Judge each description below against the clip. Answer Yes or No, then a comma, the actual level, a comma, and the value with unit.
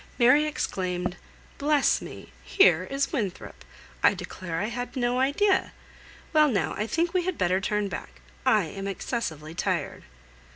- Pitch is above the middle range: Yes, high, 235 Hz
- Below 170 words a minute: Yes, average, 150 wpm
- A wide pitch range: Yes, wide, 7.5 semitones